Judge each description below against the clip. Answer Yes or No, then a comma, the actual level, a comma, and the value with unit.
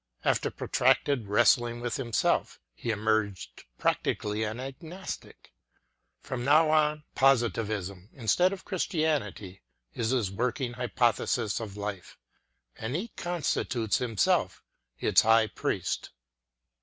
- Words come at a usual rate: No, slow, 120 wpm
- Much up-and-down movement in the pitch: No, average, 4.7 semitones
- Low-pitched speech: Yes, low, 120 Hz